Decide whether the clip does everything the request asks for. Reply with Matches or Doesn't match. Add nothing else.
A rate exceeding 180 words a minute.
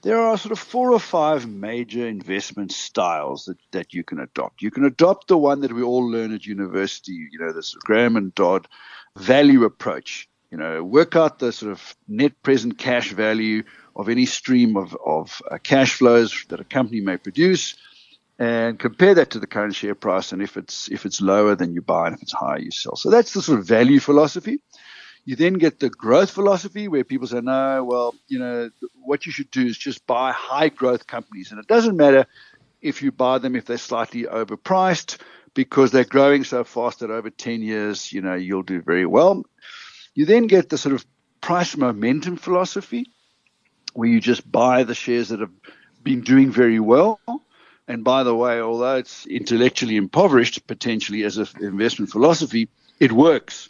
Matches